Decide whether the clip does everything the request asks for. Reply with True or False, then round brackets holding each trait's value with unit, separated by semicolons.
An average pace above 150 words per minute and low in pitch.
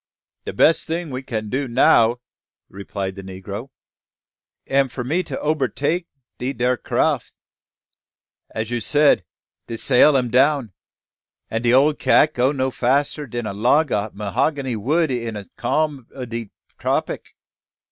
False (145 wpm; 125 Hz)